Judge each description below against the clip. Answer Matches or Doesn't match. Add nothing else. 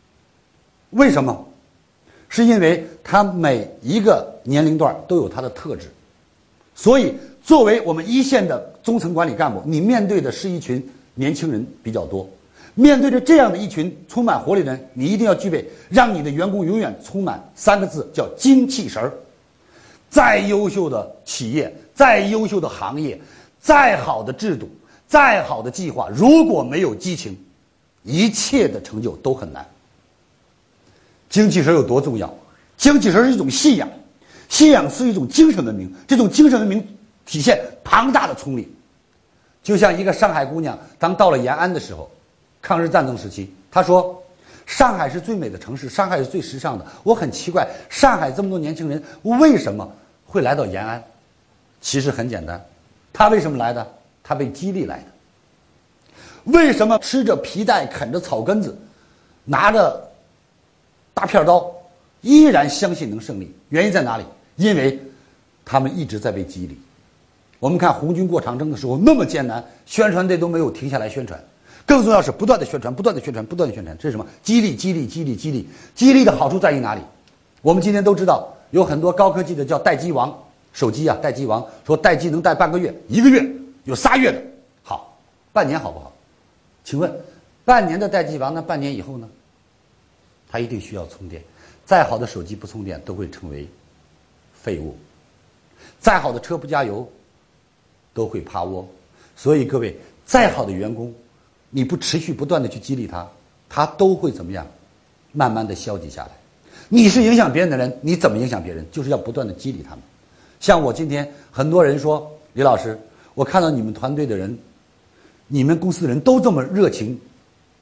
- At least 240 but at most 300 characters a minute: Matches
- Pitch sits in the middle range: Matches